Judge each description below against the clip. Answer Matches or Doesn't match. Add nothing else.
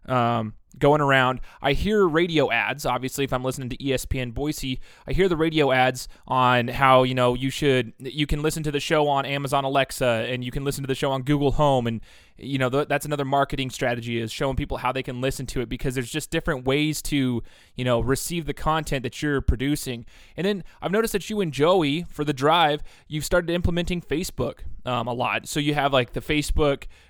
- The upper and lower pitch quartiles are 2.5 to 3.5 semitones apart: Matches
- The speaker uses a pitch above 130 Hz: Matches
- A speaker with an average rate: Doesn't match